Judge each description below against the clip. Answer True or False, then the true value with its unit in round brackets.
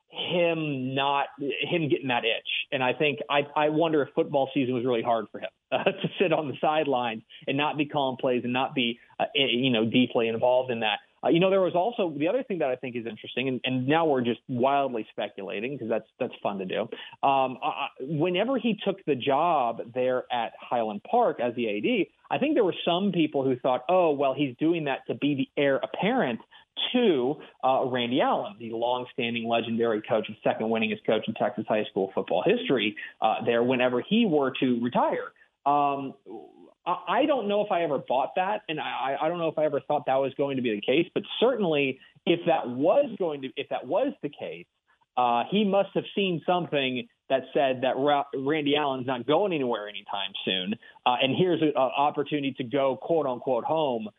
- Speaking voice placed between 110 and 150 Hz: True (140 Hz)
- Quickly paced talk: True (210 wpm)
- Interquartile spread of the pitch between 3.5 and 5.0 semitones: True (4.1 semitones)